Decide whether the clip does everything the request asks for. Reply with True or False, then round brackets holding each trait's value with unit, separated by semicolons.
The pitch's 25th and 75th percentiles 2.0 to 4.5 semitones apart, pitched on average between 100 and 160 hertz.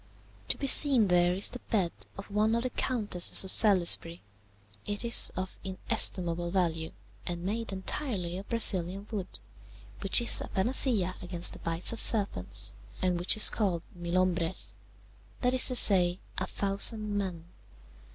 False (3.7 semitones; 190 Hz)